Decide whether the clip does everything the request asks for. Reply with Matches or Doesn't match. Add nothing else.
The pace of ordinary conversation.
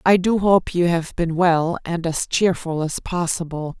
Matches